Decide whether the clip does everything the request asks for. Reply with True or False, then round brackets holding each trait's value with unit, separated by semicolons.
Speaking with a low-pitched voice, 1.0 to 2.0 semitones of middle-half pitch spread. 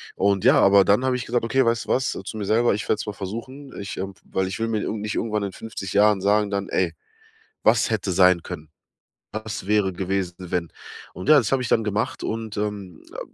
False (105 Hz; 2.6 semitones)